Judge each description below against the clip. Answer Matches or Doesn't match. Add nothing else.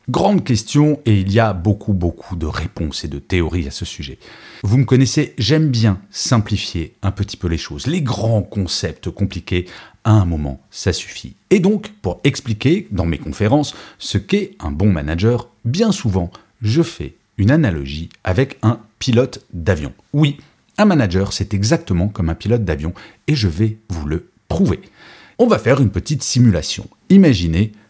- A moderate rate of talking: Matches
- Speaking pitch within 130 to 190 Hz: Doesn't match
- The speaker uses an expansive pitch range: Matches